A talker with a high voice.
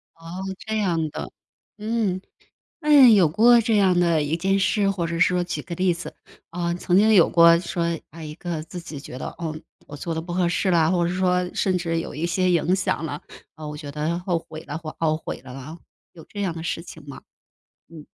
No: medium, 170 Hz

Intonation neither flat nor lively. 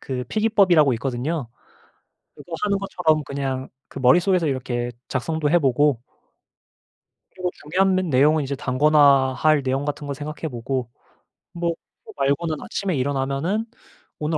Yes: average, 4.1 semitones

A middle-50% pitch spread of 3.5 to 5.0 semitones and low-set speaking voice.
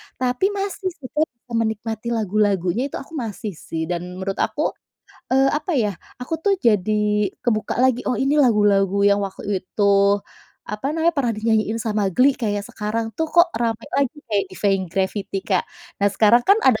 No: average, 4.2 semitones; high, 220 Hz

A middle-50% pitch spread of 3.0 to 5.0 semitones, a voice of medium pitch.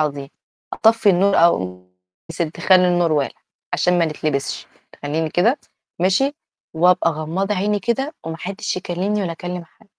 Yes: average, 3.5 semitones; medium, 180 Hz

